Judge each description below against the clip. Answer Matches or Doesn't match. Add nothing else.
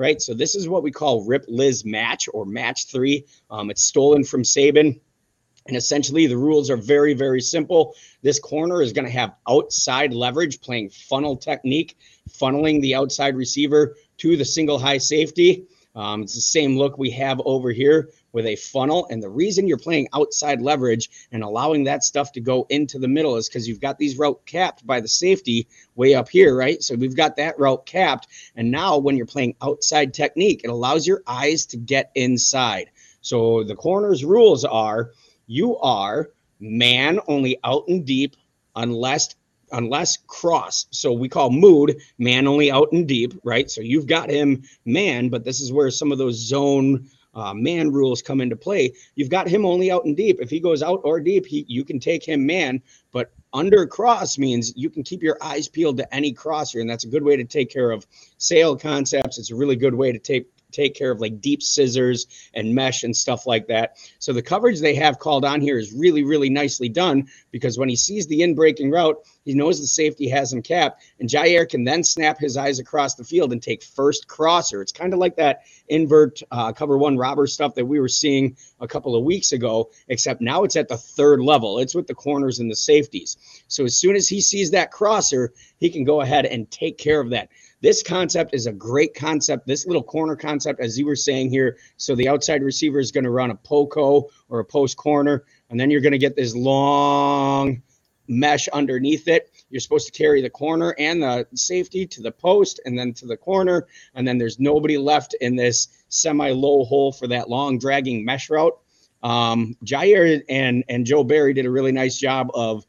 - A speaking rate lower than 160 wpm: Doesn't match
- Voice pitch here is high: Doesn't match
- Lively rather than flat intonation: Doesn't match